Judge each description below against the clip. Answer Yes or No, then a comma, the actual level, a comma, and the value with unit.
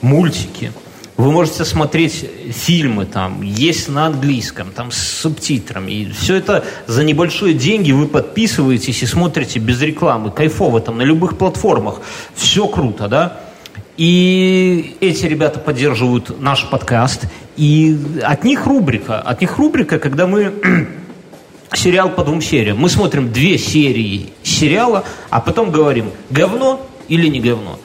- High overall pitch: No, medium, 150 Hz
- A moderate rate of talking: Yes, average, 135 wpm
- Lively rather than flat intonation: Yes, wide, 6.3 semitones